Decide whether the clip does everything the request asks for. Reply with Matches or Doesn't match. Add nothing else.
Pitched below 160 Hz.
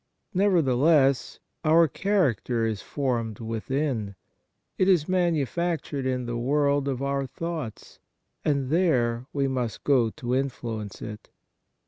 Matches